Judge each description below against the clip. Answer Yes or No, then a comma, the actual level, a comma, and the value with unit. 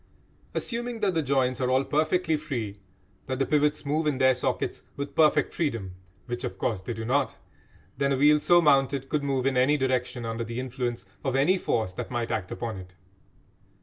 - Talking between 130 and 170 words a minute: No, average, 195 wpm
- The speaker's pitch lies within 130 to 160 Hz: Yes, low, 135 Hz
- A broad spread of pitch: No, average, 3.6 semitones